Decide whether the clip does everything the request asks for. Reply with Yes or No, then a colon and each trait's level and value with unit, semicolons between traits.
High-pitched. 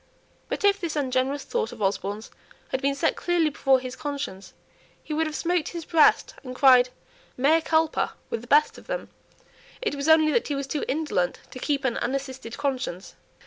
Yes: very high, 280 Hz